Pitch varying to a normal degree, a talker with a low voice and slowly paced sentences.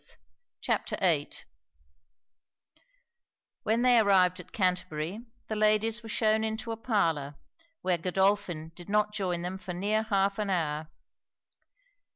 No: average, 3.6 semitones; high, 195 Hz; slow, 130 wpm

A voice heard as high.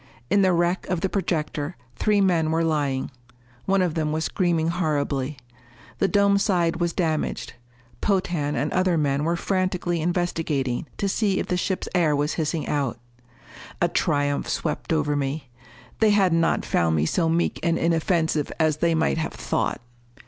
No: medium, 165 Hz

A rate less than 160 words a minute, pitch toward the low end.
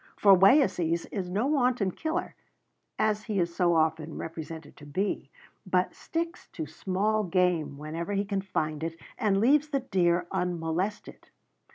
No: average, 150 wpm; medium, 185 Hz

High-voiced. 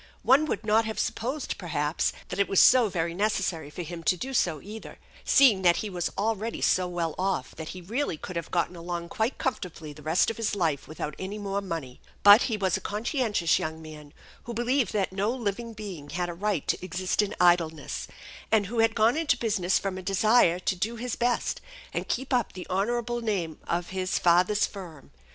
Yes: high, 195 Hz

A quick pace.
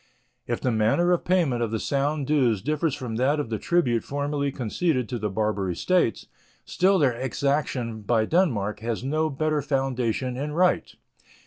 No: average, 165 wpm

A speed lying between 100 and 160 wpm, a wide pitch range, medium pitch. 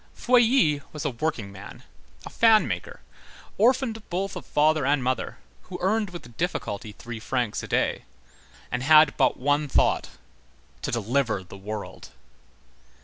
Yes: average, 140 wpm; wide, 7.6 semitones; medium, 145 Hz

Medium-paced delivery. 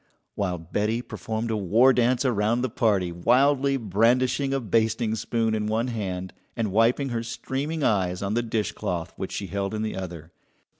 Yes: average, 170 wpm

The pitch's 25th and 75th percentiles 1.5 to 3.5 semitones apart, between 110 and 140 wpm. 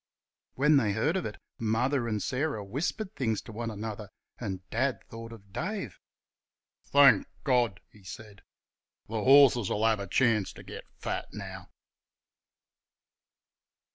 No: average, 4.4 semitones; slow, 135 wpm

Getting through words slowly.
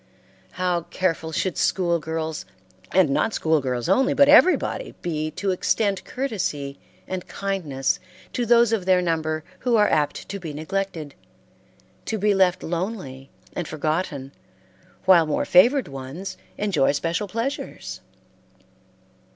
Yes: slow, 130 wpm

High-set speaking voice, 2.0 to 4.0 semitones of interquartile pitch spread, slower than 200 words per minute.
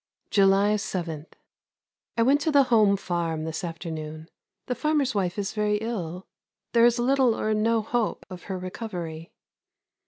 No: high, 205 Hz; average, 5.1 semitones; average, 150 wpm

